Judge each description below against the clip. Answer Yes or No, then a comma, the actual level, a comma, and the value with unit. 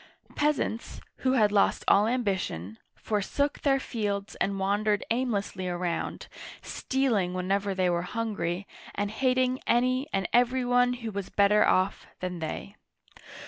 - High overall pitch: Yes, high, 205 Hz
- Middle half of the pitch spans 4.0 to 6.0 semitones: Yes, average, 4.5 semitones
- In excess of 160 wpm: No, slow, 135 wpm